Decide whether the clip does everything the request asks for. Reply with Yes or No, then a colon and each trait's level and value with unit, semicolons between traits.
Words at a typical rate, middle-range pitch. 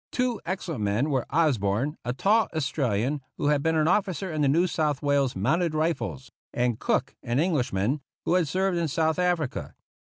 Yes: average, 180 wpm; medium, 150 Hz